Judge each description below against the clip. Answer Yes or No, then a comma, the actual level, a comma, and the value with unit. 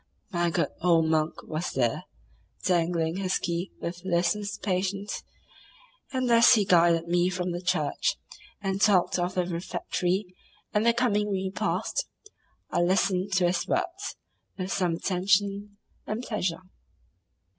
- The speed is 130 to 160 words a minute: Yes, slow, 135 wpm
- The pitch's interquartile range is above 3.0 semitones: No, average, 2.7 semitones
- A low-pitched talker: No, medium, 185 Hz